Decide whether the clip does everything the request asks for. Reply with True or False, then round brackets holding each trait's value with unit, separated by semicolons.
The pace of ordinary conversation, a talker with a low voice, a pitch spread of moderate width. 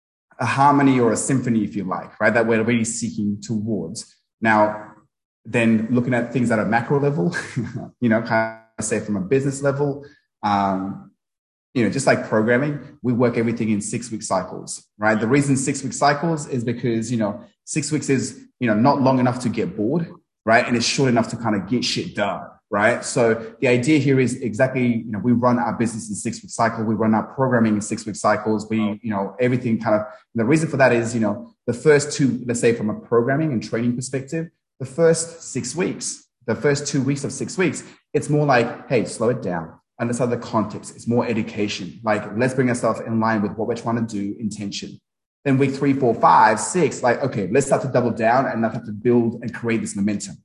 False (220 wpm; 115 Hz; 3.3 semitones)